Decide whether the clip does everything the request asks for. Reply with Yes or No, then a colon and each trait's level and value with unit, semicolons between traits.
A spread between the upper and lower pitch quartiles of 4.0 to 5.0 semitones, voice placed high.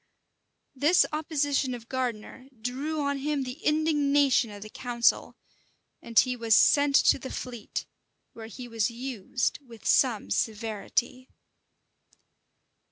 No: average, 3.5 semitones; very high, 255 Hz